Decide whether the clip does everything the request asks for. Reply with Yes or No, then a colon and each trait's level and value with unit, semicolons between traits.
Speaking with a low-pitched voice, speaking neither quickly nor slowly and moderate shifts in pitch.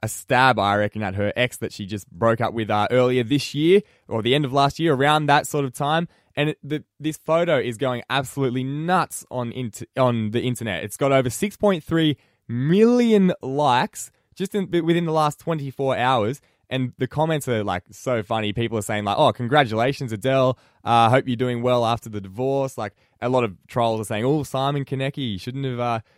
No: low, 130 Hz; fast, 210 wpm; average, 4.1 semitones